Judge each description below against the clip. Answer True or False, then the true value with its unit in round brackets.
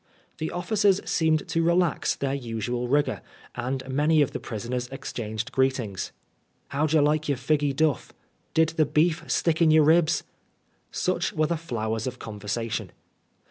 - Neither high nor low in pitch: True (145 Hz)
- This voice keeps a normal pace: True (165 wpm)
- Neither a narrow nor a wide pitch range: True (4.6 semitones)